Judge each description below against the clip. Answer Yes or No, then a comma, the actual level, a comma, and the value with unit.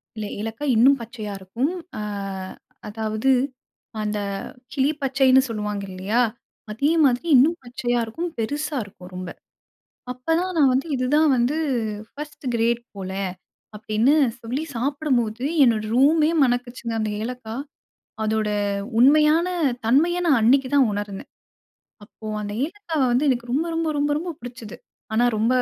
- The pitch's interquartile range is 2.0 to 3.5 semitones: No, average, 4.7 semitones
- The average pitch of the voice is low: No, very high, 250 Hz